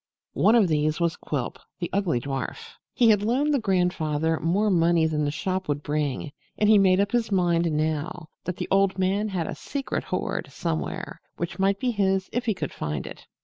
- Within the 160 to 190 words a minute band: No, average, 200 wpm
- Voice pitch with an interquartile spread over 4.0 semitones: Yes, average, 4.4 semitones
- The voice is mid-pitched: Yes, medium, 180 Hz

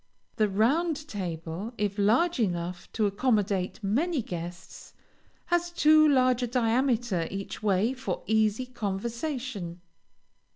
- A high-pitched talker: Yes, high, 220 Hz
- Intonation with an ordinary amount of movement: Yes, average, 5.0 semitones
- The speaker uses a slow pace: Yes, slow, 115 wpm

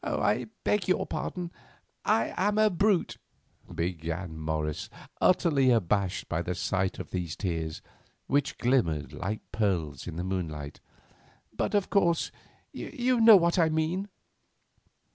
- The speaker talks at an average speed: No, slow, 130 wpm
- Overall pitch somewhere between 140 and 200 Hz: No, low, 105 Hz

